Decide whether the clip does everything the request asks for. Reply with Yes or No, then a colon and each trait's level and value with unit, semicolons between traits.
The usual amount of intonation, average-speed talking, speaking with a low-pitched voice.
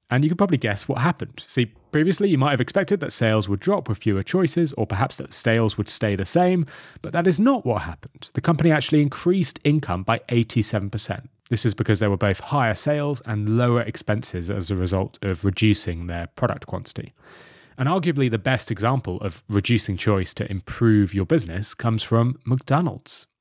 No: wide, 5.9 semitones; average, 190 wpm; low, 115 Hz